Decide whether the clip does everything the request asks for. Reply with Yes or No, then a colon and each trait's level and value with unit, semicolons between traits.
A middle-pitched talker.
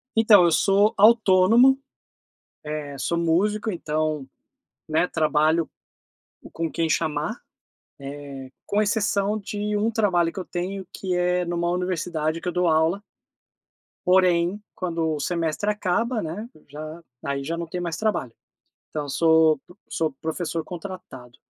Yes: medium, 175 Hz